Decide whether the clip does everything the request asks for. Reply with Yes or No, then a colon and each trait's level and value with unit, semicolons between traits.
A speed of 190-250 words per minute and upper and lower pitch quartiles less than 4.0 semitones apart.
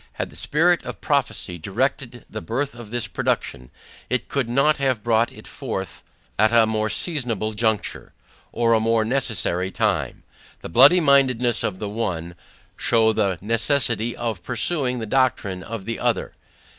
No: average, 155 wpm; average, 3.3 semitones